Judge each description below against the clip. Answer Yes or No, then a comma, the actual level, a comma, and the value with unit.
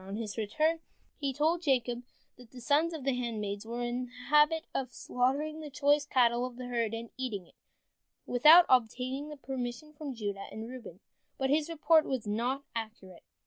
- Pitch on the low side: No, very high, 250 Hz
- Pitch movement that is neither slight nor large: Yes, average, 4.1 semitones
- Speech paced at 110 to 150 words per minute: No, average, 180 wpm